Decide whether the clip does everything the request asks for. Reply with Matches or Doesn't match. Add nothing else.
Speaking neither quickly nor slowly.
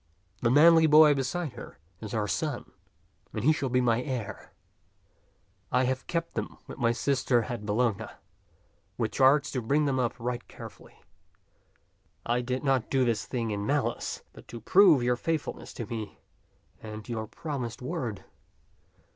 Matches